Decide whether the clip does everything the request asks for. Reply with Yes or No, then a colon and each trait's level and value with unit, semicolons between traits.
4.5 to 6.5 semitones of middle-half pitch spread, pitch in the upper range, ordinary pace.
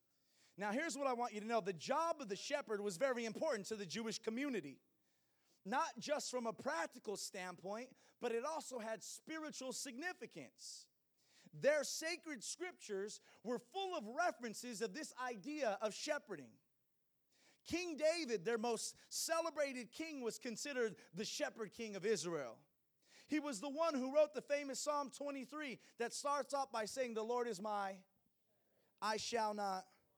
Yes: average, 5.2 semitones; high, 245 Hz; average, 155 wpm